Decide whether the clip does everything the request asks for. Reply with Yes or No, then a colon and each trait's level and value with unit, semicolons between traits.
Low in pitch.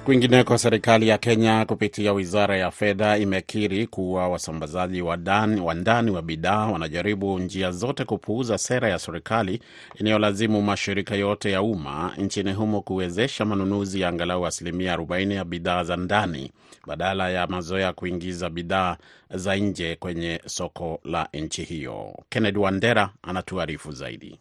Yes: very low, 95 Hz